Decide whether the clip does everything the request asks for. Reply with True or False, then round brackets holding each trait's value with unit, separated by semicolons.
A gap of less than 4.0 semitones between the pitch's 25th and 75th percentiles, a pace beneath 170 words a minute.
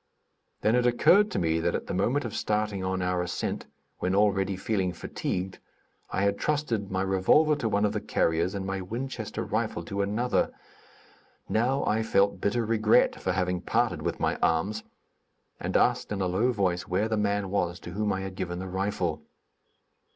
False (2.9 semitones; 185 wpm)